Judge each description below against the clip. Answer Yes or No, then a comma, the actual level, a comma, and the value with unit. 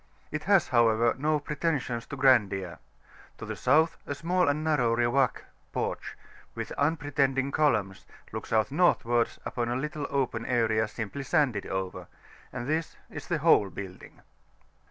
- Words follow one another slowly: No, average, 145 wpm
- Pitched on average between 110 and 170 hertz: Yes, low, 135 Hz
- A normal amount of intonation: Yes, average, 4.8 semitones